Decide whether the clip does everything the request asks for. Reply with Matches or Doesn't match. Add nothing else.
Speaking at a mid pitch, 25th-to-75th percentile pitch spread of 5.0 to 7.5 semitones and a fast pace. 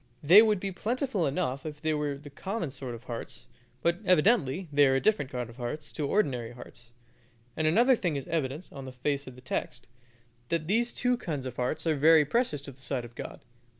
Matches